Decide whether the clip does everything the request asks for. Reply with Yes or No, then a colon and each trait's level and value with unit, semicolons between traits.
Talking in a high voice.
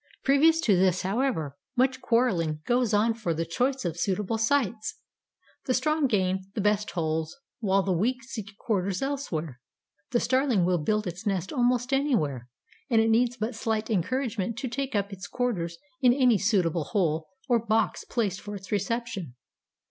Yes: high, 215 Hz